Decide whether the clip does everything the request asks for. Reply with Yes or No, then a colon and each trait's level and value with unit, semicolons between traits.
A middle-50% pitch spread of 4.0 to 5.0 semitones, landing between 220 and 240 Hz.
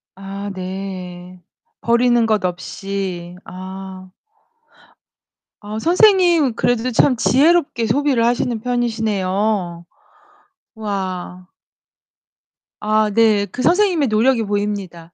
No: average, 4.4 semitones; high, 210 Hz